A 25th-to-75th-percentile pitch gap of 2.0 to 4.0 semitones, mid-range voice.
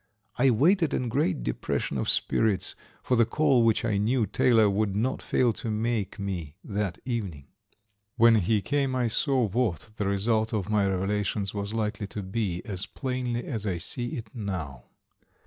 No: average, 3.4 semitones; low, 110 Hz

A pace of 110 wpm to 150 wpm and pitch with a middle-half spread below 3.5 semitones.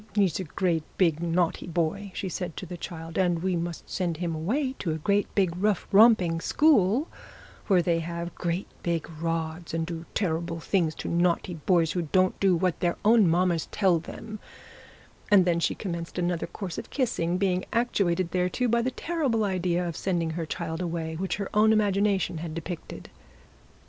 No: average, 180 wpm; average, 2.9 semitones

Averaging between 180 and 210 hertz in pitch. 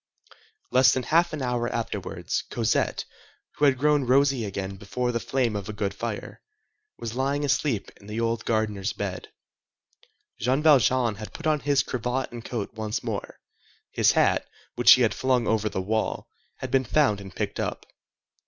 No: low, 120 Hz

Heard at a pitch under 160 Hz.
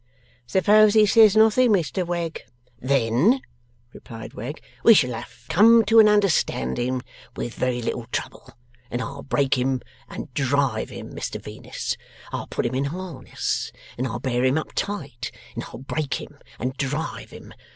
Yes: medium, 140 Hz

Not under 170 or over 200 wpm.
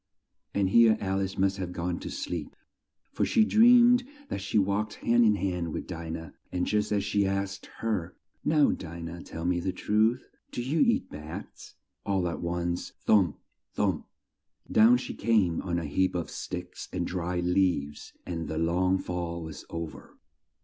Yes: average, 175 wpm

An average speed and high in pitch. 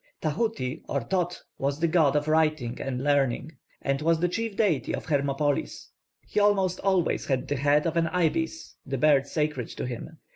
No: average, 180 wpm; medium, 155 Hz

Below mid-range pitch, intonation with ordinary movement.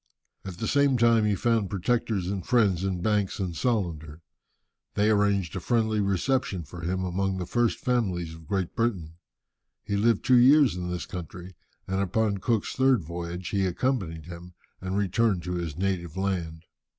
Yes: very low, 95 Hz; average, 4.2 semitones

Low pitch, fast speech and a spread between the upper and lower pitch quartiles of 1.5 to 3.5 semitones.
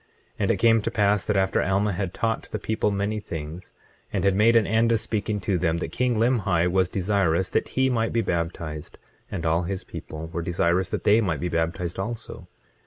No: very low, 95 Hz; fast, 215 wpm; average, 4.3 semitones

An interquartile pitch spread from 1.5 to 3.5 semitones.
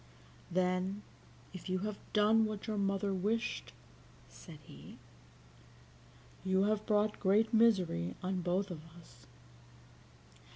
Yes: narrow, 2.6 semitones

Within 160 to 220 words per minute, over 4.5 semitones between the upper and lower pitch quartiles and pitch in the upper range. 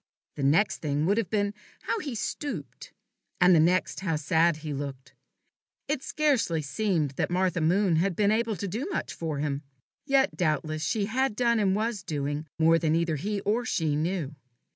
No: average, 185 wpm; wide, 5.5 semitones; medium, 180 Hz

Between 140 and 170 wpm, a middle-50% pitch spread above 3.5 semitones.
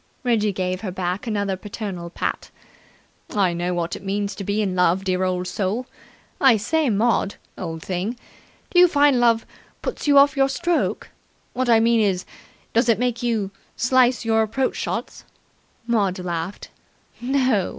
Yes: average, 160 wpm; average, 4.7 semitones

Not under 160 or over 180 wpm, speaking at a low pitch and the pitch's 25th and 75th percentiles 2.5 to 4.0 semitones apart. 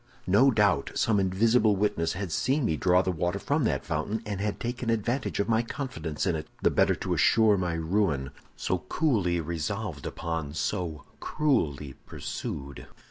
No: average, 165 wpm; very low, 95 Hz; wide, 5.4 semitones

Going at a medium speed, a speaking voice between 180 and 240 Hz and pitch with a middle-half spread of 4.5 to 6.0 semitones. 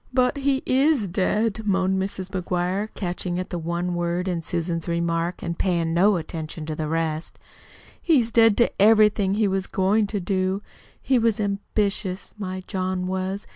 No: average, 165 wpm; high, 190 Hz; average, 3.3 semitones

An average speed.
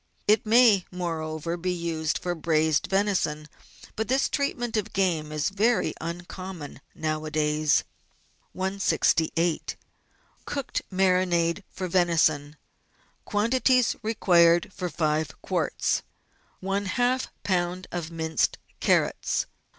No: slow, 95 wpm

